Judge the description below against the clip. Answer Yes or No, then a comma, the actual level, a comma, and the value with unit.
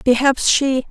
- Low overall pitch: No, very high, 265 Hz